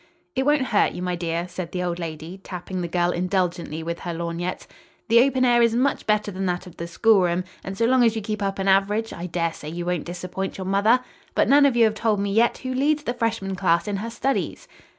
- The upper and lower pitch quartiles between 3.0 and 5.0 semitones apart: Yes, average, 4.6 semitones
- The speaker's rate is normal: No, fast, 240 wpm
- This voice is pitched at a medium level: No, high, 195 Hz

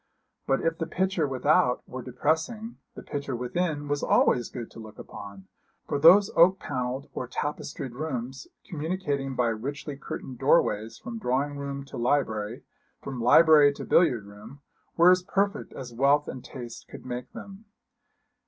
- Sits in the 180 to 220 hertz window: No, medium, 140 Hz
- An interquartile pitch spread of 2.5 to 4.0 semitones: No, average, 4.5 semitones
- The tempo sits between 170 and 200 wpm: No, average, 155 wpm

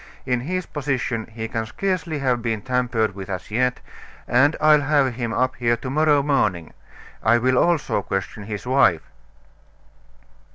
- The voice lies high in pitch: No, low, 125 Hz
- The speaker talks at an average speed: Yes, average, 155 wpm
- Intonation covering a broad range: No, average, 4.2 semitones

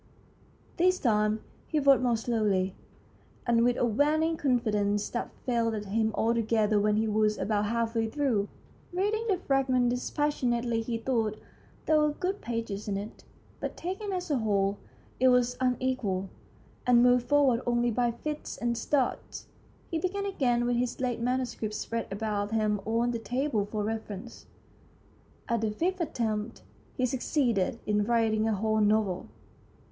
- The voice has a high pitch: Yes, high, 235 Hz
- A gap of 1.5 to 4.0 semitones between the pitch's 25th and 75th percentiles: Yes, average, 3.3 semitones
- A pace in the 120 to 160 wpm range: Yes, average, 155 wpm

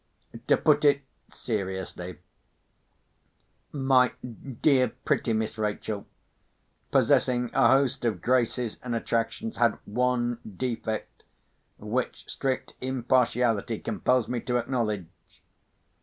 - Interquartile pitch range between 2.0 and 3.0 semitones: Yes, narrow, 2.6 semitones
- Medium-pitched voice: No, low, 120 Hz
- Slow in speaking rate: Yes, slow, 95 wpm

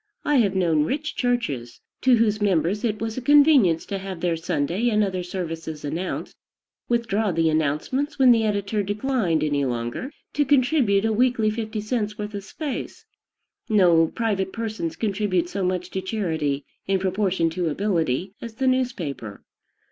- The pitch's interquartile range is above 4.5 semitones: Yes, wide, 5.6 semitones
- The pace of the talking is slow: No, average, 160 wpm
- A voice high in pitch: Yes, high, 200 Hz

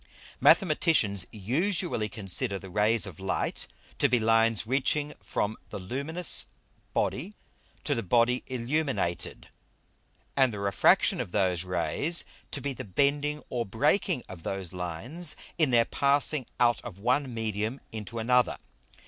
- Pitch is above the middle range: No, low, 115 Hz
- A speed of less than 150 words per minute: Yes, average, 140 wpm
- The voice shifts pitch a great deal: Yes, wide, 6.0 semitones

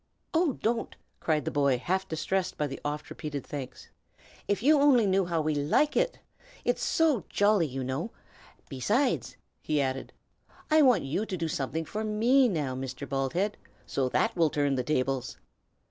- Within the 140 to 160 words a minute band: No, average, 170 wpm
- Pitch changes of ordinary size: No, wide, 7.8 semitones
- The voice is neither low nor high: Yes, medium, 160 Hz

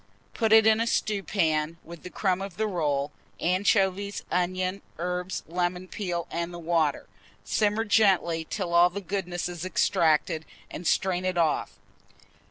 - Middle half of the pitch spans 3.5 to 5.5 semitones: No, narrow, 2.6 semitones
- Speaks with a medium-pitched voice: Yes, medium, 180 Hz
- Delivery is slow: No, average, 150 wpm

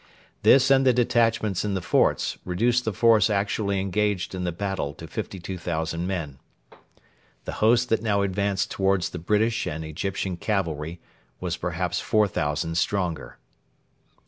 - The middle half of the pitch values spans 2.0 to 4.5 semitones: Yes, average, 3.7 semitones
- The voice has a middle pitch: No, very low, 95 Hz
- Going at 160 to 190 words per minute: No, average, 140 wpm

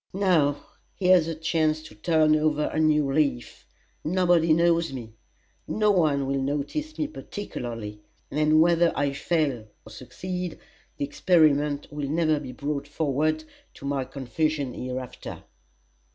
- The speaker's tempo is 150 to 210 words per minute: No, slow, 135 wpm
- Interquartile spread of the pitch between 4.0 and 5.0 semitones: No, average, 3.0 semitones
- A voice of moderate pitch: Yes, medium, 150 Hz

